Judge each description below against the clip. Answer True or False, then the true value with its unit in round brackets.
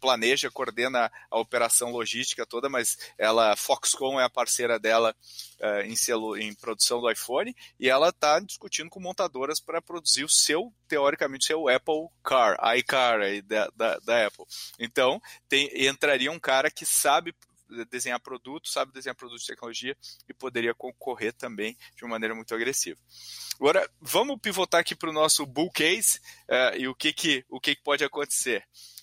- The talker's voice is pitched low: True (130 Hz)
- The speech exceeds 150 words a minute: True (170 wpm)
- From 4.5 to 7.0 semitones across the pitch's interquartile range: True (5.1 semitones)